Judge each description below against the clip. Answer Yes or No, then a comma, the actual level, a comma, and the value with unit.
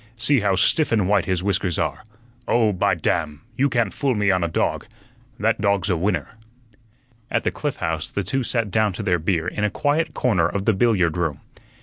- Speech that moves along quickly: Yes, fast, 210 wpm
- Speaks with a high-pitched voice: No, low, 100 Hz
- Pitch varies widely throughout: No, average, 4.2 semitones